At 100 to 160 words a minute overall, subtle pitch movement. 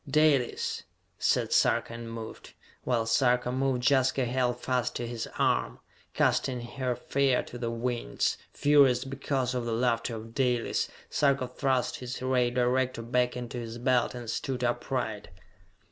Yes: average, 145 wpm; narrow, 1.7 semitones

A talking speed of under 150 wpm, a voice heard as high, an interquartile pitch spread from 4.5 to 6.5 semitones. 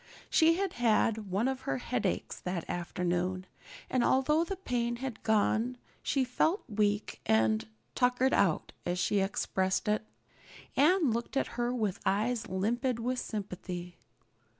Yes: average, 140 wpm; high, 225 Hz; average, 5.1 semitones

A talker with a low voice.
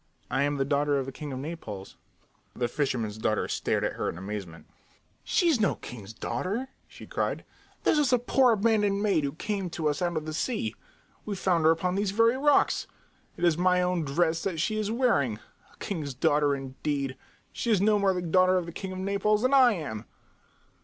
No: medium, 170 Hz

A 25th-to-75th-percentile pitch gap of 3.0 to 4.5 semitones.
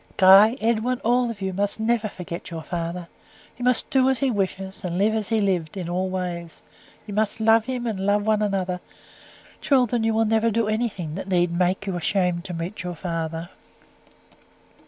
Yes: average, 3.8 semitones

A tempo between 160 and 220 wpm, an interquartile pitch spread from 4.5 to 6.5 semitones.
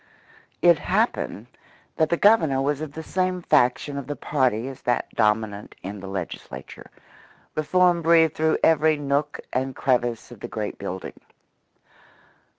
No: average, 145 wpm; average, 5.2 semitones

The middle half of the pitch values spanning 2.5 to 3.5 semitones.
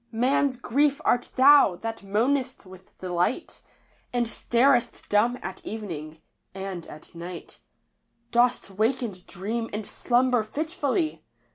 No: average, 5.1 semitones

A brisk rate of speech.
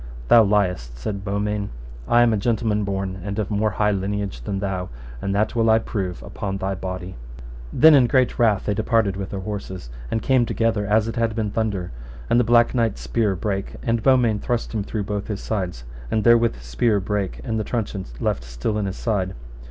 Yes: fast, 210 wpm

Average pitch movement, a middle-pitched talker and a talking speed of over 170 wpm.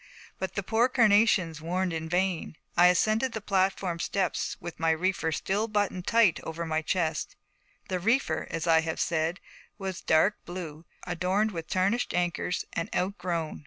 No: average, 3.3 semitones; medium, 180 Hz; average, 160 wpm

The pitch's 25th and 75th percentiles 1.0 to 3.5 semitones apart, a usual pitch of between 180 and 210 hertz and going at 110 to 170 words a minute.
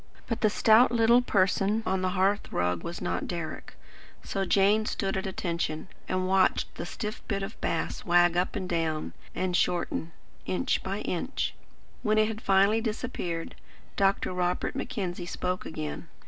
Yes: average, 3.2 semitones; high, 190 Hz; average, 160 wpm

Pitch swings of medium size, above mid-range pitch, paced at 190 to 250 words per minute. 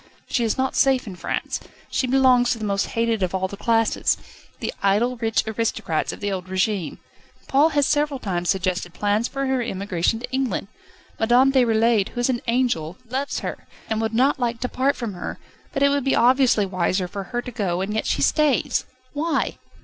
Yes: average, 4.7 semitones; high, 230 Hz; average, 200 wpm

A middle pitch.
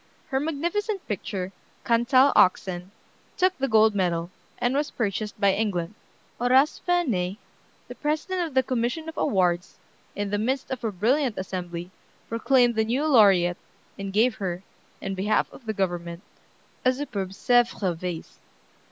No: high, 220 Hz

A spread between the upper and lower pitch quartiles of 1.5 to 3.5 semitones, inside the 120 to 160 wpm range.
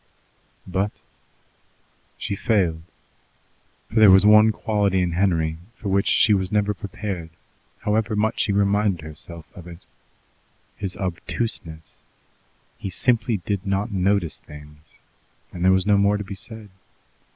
Yes: average, 2.8 semitones; slow, 135 wpm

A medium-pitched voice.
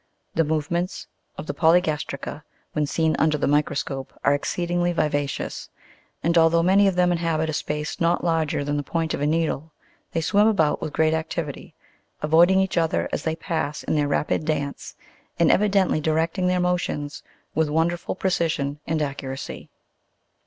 Yes: medium, 160 Hz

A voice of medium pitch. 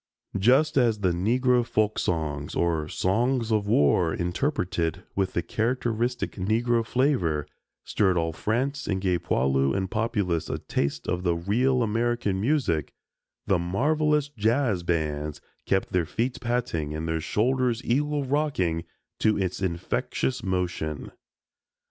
No: low, 100 Hz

